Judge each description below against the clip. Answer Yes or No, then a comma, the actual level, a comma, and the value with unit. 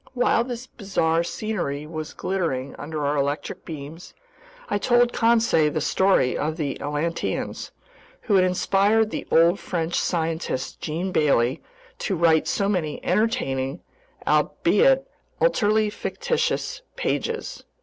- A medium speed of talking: No, slow, 115 wpm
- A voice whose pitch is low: No, medium, 175 Hz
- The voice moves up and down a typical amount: No, wide, 6.4 semitones